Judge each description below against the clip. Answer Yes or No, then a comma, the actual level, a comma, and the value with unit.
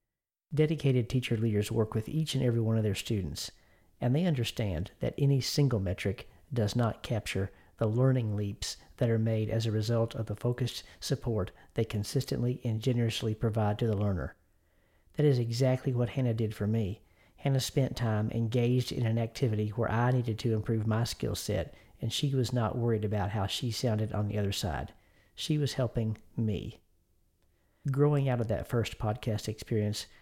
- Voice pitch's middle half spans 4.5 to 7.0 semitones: No, average, 2.9 semitones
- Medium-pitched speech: No, low, 115 Hz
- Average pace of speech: Yes, average, 180 wpm